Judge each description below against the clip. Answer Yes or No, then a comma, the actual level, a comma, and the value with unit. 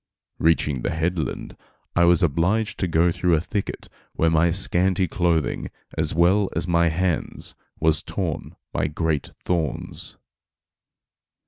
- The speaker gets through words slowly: Yes, slow, 130 wpm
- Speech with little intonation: Yes, narrow, 2.0 semitones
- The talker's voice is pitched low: Yes, very low, 85 Hz